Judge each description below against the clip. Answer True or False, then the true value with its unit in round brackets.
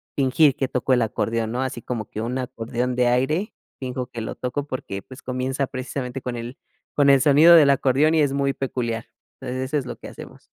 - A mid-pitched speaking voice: False (130 Hz)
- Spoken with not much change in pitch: True (2.1 semitones)